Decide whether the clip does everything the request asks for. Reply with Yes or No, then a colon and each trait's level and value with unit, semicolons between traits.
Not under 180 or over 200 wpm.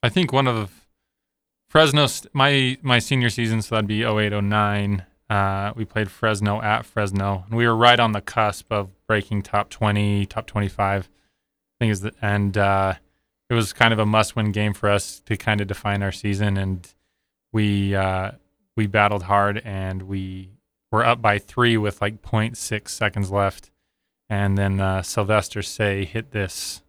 Yes: average, 185 wpm